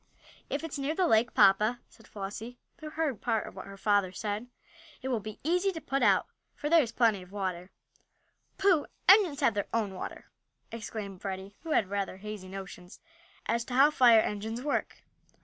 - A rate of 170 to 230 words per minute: Yes, average, 190 wpm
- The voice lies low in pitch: No, high, 220 Hz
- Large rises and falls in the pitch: Yes, wide, 6.0 semitones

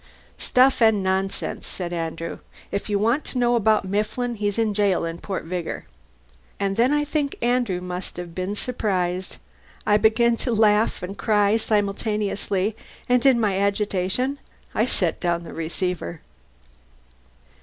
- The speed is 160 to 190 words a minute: No, average, 145 wpm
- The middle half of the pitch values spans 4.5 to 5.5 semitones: No, average, 3.8 semitones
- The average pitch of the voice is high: Yes, high, 205 Hz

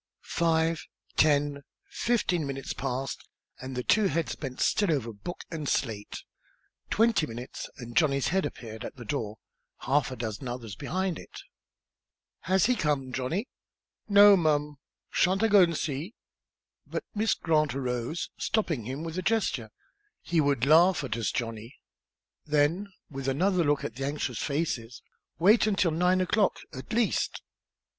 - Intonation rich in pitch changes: Yes, wide, 5.9 semitones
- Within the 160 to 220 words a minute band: No, average, 150 wpm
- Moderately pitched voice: Yes, medium, 150 Hz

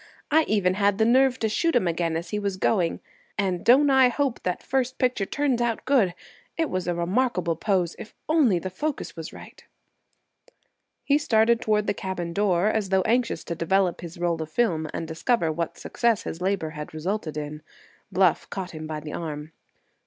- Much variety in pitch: Yes, wide, 5.8 semitones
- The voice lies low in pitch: No, high, 190 Hz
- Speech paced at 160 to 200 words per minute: Yes, average, 190 wpm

